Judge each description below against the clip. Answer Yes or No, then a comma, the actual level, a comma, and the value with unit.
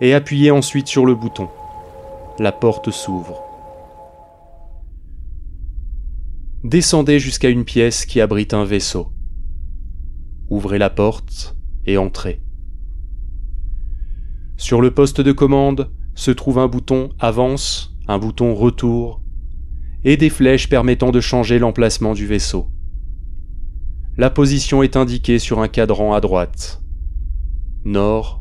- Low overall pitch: Yes, low, 100 Hz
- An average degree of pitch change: No, wide, 8.2 semitones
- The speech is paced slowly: Yes, slow, 115 wpm